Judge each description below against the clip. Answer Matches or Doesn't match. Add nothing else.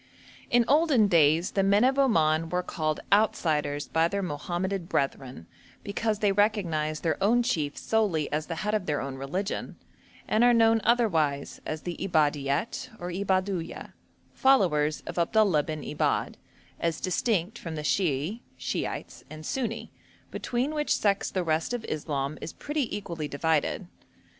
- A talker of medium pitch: Matches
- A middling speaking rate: Matches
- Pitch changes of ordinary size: Doesn't match